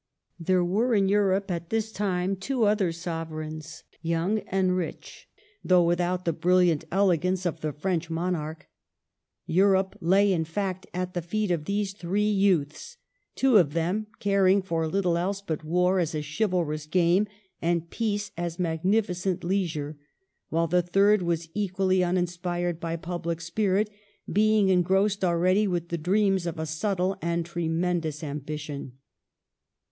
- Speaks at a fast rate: No, average, 145 wpm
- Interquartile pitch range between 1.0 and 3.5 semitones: Yes, average, 2.8 semitones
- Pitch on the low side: No, medium, 180 Hz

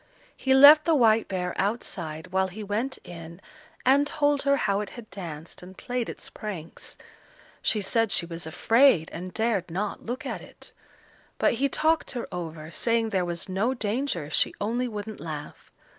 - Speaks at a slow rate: No, average, 175 wpm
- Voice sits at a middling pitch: No, high, 210 Hz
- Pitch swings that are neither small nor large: No, wide, 5.9 semitones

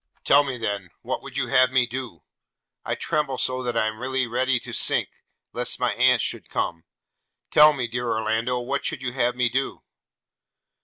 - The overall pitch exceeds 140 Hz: No, low, 125 Hz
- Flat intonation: Yes, narrow, 1.8 semitones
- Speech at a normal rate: Yes, average, 190 wpm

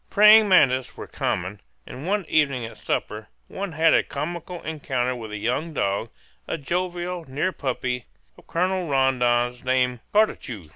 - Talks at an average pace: Yes, average, 150 wpm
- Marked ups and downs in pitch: Yes, wide, 6.0 semitones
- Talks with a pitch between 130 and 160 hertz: Yes, medium, 140 Hz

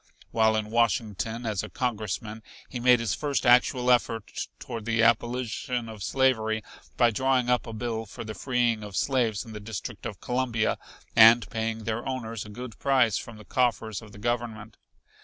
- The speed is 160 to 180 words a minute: Yes, average, 175 wpm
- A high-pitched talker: No, low, 115 Hz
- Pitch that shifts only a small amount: Yes, narrow, 2.0 semitones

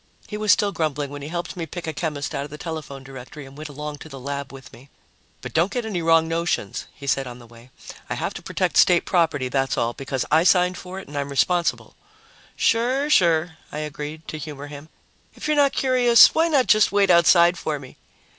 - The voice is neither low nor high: Yes, medium, 155 Hz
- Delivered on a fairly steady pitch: No, average, 4.3 semitones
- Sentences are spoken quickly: Yes, fast, 225 wpm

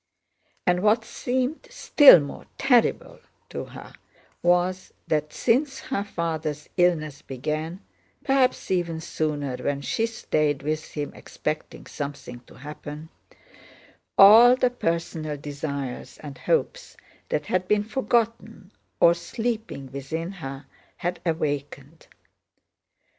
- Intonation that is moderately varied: No, wide, 6.3 semitones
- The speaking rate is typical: No, slow, 110 wpm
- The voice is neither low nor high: Yes, medium, 165 Hz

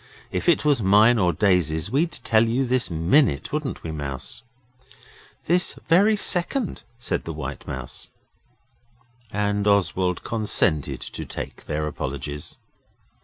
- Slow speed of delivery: Yes, slow, 125 wpm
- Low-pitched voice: Yes, low, 100 Hz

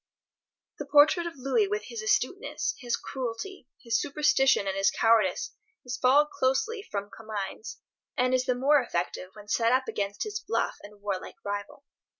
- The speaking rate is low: No, average, 165 wpm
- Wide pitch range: Yes, wide, 6.0 semitones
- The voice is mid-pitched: No, very high, 255 Hz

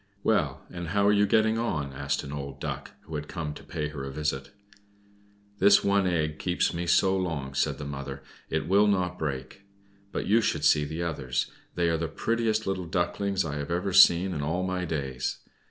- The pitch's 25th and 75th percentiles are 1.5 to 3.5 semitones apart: No, average, 4.8 semitones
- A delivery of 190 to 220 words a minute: Yes, average, 200 wpm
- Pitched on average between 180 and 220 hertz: No, very low, 85 Hz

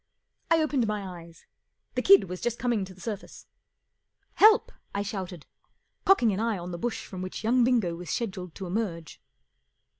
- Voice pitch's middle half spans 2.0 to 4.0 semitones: No, average, 4.7 semitones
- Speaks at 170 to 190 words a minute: Yes, average, 185 wpm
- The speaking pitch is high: Yes, high, 200 Hz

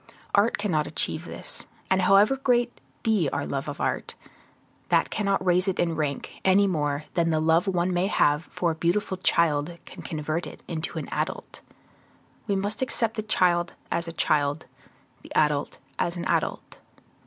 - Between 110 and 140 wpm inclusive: No, average, 170 wpm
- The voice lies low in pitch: No, medium, 175 Hz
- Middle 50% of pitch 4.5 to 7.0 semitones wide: No, average, 4.1 semitones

